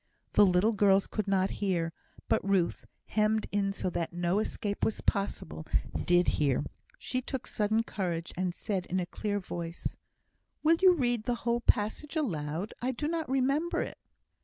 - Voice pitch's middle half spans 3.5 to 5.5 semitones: Yes, average, 5.0 semitones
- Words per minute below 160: No, average, 165 wpm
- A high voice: Yes, high, 205 Hz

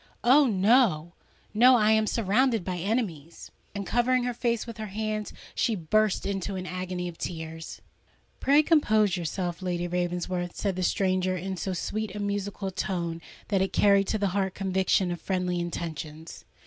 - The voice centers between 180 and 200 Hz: Yes, high, 190 Hz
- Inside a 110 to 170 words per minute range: Yes, average, 165 wpm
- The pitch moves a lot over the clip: No, average, 3.3 semitones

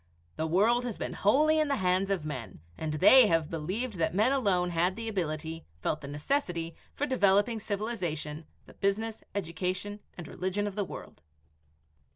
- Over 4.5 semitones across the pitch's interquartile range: Yes, average, 5.2 semitones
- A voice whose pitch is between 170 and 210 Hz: Yes, high, 190 Hz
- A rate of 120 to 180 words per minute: Yes, average, 170 wpm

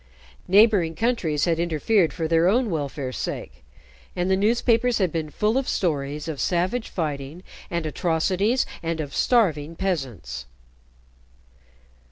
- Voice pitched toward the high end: No, medium, 170 Hz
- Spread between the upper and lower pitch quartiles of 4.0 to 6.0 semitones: Yes, average, 5.2 semitones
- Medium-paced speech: No, slow, 130 wpm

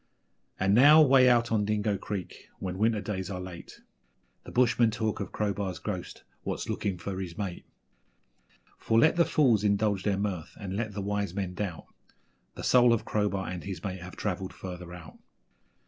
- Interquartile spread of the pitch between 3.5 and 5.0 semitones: No, average, 2.8 semitones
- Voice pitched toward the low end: Yes, low, 100 Hz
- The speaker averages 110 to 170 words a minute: No, average, 180 wpm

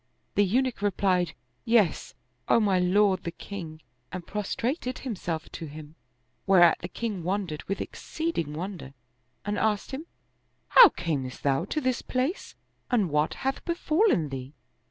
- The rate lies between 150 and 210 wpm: No, average, 140 wpm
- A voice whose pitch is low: No, high, 195 Hz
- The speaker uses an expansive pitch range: Yes, wide, 6.3 semitones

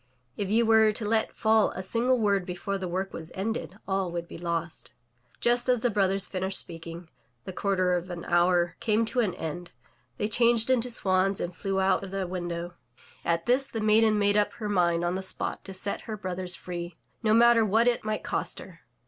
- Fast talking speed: Yes, fast, 210 wpm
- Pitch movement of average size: Yes, average, 3.8 semitones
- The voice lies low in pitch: No, high, 195 Hz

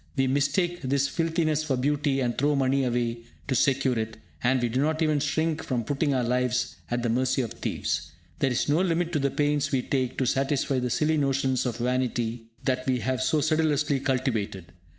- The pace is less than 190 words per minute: No, average, 200 wpm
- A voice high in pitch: No, low, 135 Hz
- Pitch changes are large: No, average, 2.8 semitones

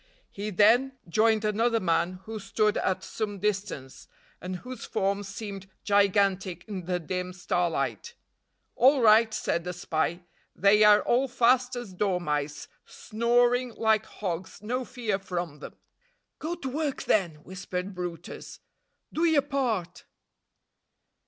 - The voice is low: No, high, 205 Hz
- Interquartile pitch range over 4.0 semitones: Yes, average, 4.4 semitones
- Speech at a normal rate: No, slow, 130 wpm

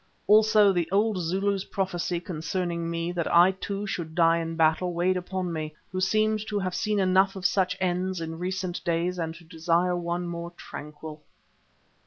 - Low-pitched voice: No, medium, 180 Hz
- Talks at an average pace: Yes, average, 175 wpm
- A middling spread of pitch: No, narrow, 2.1 semitones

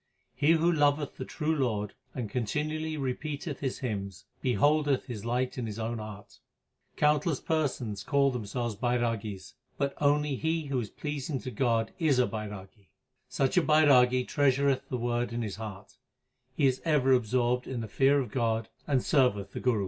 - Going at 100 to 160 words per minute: No, average, 170 wpm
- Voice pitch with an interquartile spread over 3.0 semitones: Yes, average, 4.3 semitones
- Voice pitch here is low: Yes, low, 125 Hz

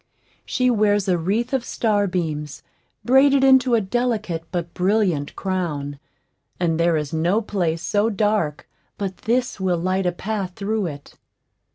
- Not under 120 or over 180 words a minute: Yes, average, 145 wpm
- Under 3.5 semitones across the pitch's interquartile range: No, average, 4.6 semitones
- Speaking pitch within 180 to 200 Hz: Yes, high, 190 Hz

